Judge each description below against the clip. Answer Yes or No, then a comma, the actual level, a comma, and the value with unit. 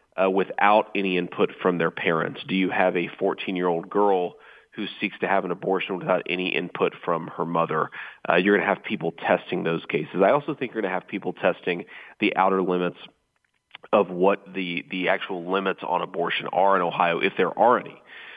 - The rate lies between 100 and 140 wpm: No, fast, 205 wpm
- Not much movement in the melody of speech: Yes, narrow, 1.9 semitones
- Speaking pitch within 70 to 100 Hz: Yes, very low, 90 Hz